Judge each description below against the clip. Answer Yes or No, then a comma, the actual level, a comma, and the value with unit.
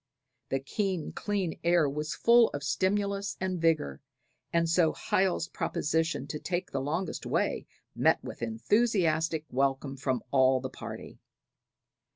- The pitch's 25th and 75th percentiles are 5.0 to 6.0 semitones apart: Yes, average, 5.3 semitones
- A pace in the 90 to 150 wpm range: Yes, slow, 135 wpm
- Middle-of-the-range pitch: Yes, medium, 160 Hz